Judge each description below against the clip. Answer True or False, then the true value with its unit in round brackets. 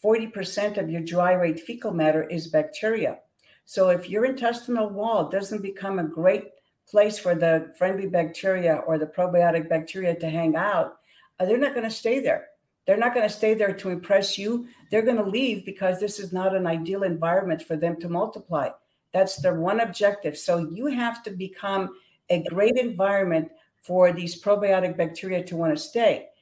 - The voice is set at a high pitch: True (195 Hz)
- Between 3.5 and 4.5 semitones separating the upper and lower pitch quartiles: True (3.9 semitones)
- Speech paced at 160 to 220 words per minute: True (180 wpm)